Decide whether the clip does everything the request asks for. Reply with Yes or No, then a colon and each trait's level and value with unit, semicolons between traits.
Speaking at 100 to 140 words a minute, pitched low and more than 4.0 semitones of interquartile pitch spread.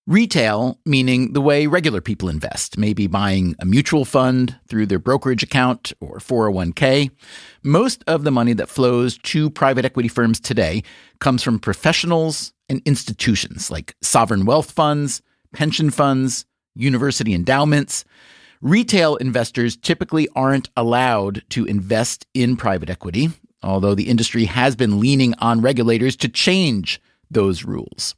Yes: slow, 135 wpm; low, 125 Hz; average, 4.4 semitones